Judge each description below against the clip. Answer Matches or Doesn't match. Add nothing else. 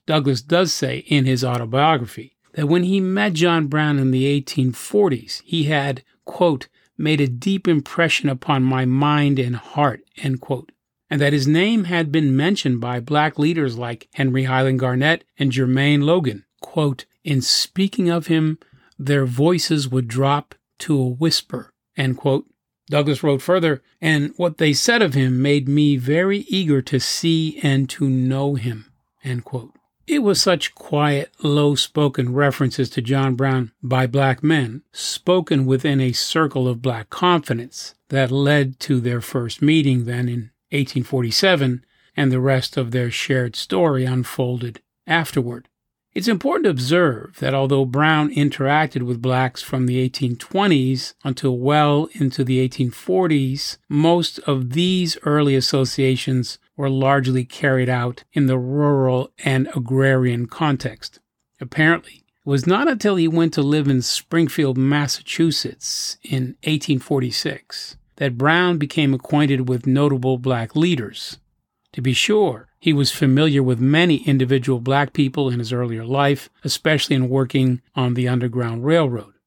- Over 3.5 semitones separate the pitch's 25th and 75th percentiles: Doesn't match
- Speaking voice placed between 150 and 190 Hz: Doesn't match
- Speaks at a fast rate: Doesn't match